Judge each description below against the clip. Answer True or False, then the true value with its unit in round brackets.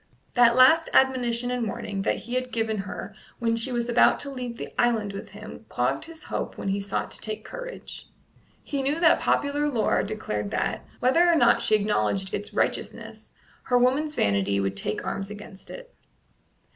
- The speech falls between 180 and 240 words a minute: True (185 wpm)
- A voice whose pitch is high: True (235 Hz)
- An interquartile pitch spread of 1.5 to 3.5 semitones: False (4.8 semitones)